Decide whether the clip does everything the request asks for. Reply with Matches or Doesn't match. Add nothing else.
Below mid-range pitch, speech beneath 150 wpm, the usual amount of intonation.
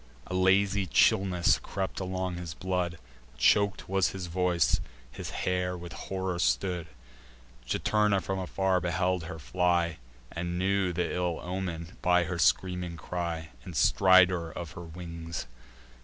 Doesn't match